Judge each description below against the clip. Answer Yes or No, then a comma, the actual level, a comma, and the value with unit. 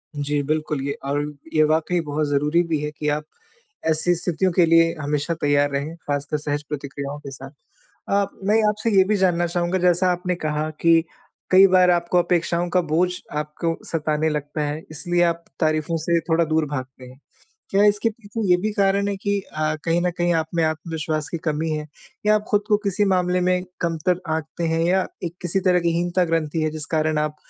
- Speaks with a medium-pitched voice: Yes, medium, 165 Hz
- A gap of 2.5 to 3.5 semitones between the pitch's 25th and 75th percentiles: Yes, average, 2.9 semitones